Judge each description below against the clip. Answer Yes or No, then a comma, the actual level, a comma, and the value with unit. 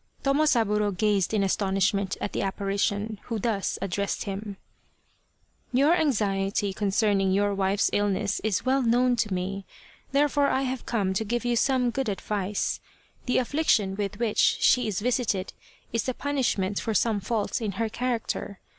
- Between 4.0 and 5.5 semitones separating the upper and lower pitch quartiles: No, average, 3.6 semitones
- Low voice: No, high, 210 Hz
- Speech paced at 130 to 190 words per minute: Yes, average, 160 wpm